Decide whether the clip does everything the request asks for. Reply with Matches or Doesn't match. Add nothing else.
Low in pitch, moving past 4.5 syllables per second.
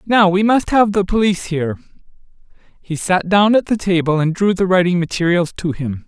Doesn't match